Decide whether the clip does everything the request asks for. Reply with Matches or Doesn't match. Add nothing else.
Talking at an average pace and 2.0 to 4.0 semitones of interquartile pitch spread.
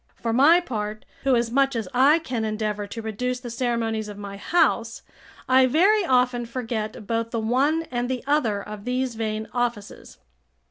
Matches